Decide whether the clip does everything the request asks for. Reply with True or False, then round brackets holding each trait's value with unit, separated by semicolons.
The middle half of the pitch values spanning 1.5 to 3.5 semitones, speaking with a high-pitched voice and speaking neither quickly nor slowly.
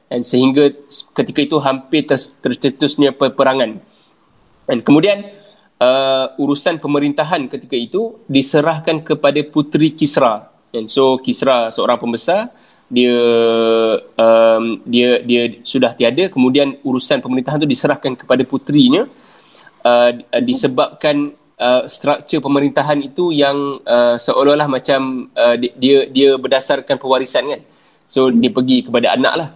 False (3.0 semitones; 135 Hz; 120 wpm)